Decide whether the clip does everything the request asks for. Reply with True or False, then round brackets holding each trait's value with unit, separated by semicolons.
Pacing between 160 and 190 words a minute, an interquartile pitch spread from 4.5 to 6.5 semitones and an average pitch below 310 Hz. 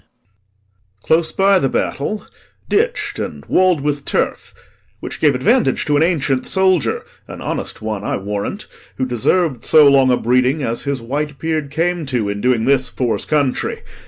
True (165 wpm; 5.3 semitones; 140 Hz)